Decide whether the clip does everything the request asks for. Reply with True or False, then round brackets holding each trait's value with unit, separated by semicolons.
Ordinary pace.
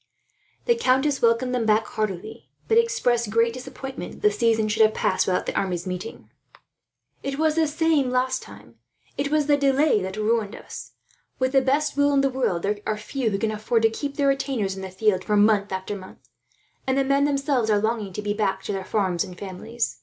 False (215 wpm)